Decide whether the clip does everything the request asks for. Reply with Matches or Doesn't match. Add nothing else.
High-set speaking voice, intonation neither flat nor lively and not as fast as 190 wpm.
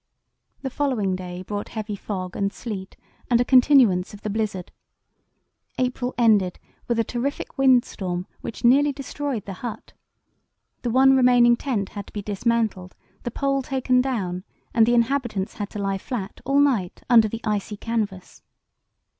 Matches